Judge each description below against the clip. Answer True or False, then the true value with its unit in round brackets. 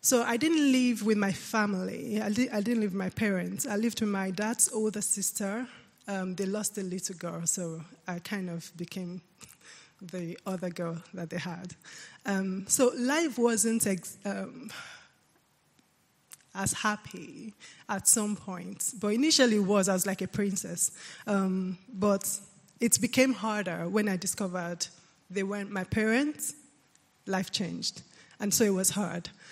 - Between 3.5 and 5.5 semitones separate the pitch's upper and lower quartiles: False (3.1 semitones)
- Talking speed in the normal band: True (160 wpm)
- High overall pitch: True (200 Hz)